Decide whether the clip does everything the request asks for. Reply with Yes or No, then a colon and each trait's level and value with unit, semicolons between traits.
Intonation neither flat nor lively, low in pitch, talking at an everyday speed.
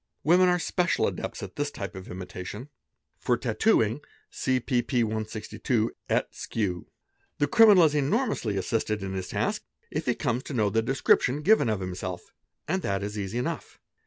No: wide, 6.4 semitones; low, 115 Hz; average, 165 wpm